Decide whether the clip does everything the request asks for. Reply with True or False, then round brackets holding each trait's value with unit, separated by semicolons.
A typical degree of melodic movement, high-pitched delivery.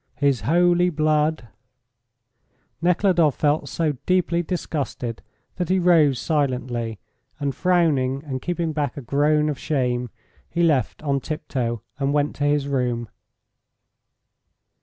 False (4.2 semitones; 145 Hz)